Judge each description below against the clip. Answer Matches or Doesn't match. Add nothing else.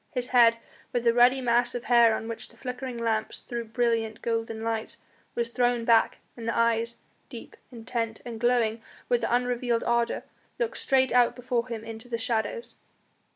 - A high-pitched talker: Matches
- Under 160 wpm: Doesn't match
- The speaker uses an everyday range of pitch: Doesn't match